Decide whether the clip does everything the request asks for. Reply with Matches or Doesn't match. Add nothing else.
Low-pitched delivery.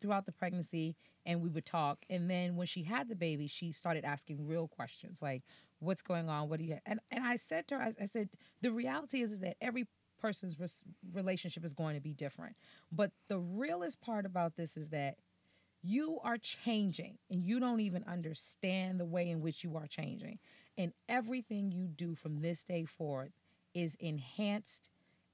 Doesn't match